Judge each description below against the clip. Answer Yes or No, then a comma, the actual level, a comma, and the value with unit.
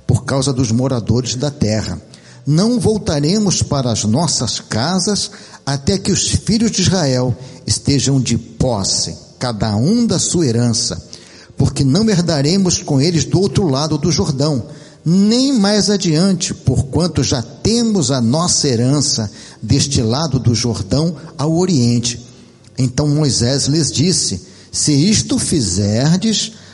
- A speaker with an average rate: Yes, average, 130 wpm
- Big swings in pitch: Yes, wide, 6.3 semitones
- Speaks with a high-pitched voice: No, medium, 140 Hz